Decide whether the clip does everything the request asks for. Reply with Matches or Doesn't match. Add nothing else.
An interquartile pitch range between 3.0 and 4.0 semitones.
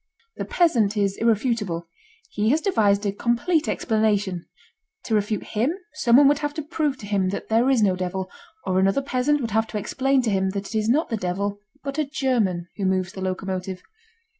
Doesn't match